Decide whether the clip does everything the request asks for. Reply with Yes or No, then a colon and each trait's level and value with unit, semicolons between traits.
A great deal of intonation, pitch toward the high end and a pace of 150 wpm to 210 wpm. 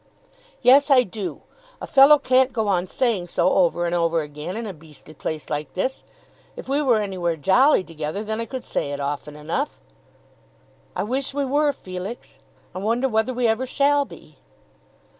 Yes: wide, 7.4 semitones; high, 210 Hz; average, 180 wpm